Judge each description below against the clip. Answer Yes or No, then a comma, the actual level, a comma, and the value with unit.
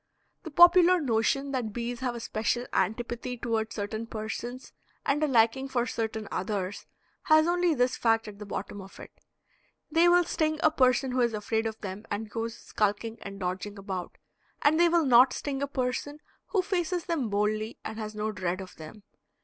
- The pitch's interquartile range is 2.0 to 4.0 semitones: No, average, 4.8 semitones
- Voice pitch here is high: Yes, high, 230 Hz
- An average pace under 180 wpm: No, average, 185 wpm